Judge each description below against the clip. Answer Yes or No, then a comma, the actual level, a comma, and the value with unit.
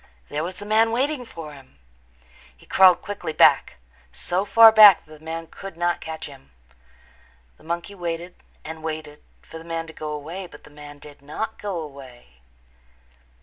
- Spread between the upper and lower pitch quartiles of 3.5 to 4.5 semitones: Yes, average, 4.1 semitones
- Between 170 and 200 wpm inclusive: Yes, average, 175 wpm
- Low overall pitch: No, medium, 165 Hz